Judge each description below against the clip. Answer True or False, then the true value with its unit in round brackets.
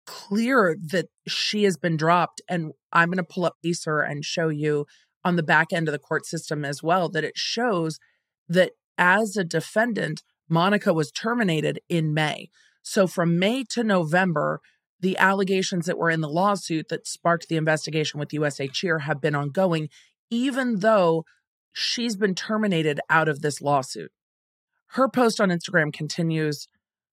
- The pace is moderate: True (165 wpm)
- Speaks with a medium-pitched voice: True (170 Hz)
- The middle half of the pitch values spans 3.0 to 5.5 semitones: True (3.7 semitones)